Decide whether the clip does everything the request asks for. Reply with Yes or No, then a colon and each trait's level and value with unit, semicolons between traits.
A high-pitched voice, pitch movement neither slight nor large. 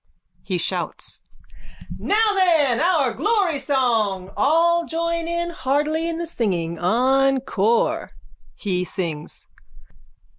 No: very high, 270 Hz; wide, 8.0 semitones